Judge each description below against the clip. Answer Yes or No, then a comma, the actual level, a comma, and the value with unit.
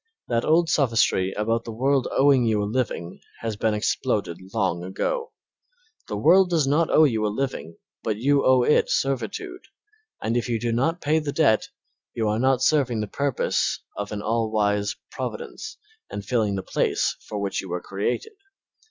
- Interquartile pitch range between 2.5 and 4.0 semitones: No, average, 5.1 semitones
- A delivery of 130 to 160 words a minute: No, average, 180 wpm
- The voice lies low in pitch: Yes, low, 115 Hz